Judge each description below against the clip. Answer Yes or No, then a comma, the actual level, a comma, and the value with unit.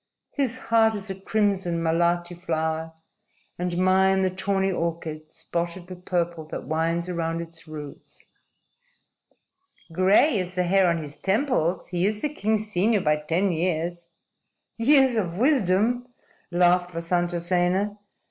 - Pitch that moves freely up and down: No, average, 2.9 semitones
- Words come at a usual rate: No, slow, 130 wpm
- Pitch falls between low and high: Yes, medium, 180 Hz